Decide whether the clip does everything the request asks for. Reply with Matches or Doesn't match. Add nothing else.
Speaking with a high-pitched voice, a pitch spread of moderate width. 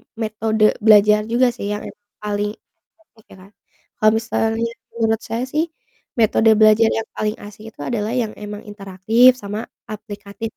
Doesn't match